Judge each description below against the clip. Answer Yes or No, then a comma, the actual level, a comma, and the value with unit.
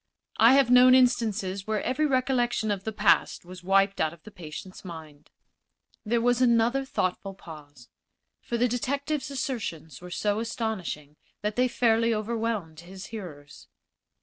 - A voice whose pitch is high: Yes, high, 215 Hz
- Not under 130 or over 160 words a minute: Yes, average, 150 wpm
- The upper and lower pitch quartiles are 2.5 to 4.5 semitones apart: No, average, 5.3 semitones